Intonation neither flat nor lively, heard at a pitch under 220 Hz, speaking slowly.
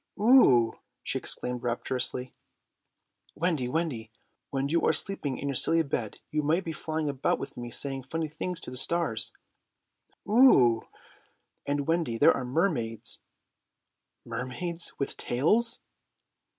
Yes: average, 5.0 semitones; medium, 140 Hz; slow, 130 wpm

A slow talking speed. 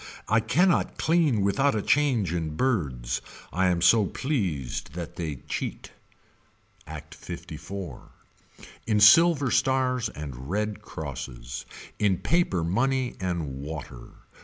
Yes: slow, 115 wpm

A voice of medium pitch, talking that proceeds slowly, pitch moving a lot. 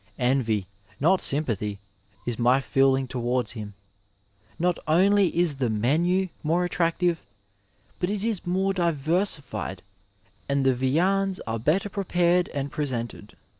Yes: medium, 150 Hz; slow, 130 wpm; wide, 6.1 semitones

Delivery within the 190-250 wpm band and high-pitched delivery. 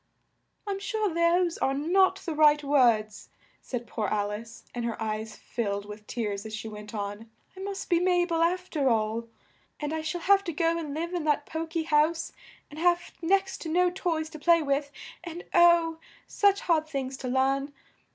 Yes: average, 195 wpm; very high, 310 Hz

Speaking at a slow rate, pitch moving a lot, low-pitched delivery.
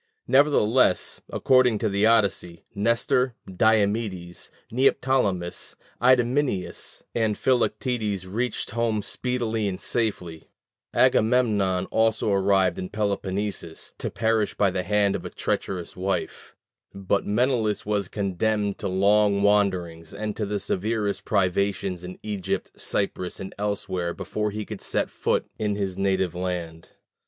No: slow, 125 wpm; average, 3.0 semitones; low, 100 Hz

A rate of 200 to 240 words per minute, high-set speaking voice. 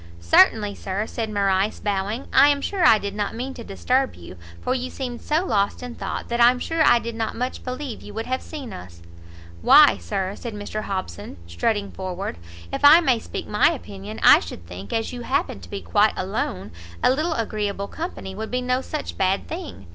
Yes: fast, 205 wpm; high, 220 Hz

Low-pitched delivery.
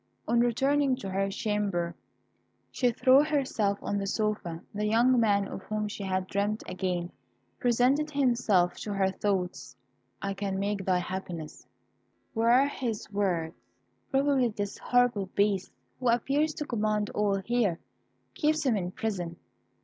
No: high, 210 Hz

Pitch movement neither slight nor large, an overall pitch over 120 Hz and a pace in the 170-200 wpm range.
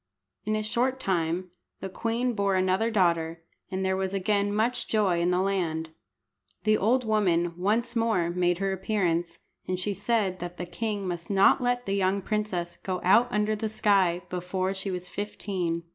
Yes: average, 3.2 semitones; high, 190 Hz; average, 175 wpm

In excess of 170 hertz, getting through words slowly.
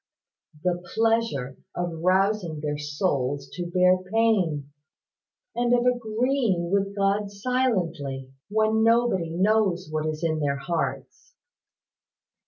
Yes: medium, 185 Hz; slow, 110 wpm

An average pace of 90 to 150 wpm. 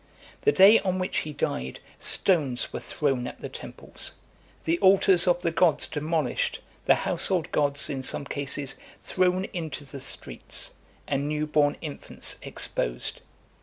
Yes: average, 145 wpm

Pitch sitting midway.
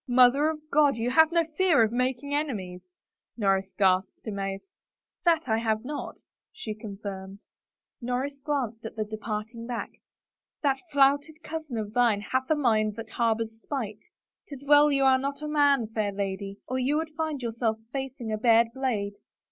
No: high, 245 Hz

